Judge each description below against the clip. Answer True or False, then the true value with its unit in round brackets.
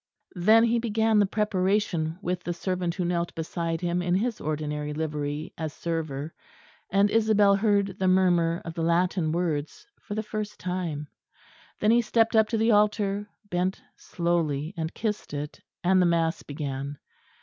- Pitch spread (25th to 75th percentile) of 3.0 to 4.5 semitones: True (4.2 semitones)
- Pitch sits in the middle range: True (180 Hz)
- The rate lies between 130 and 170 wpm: True (160 wpm)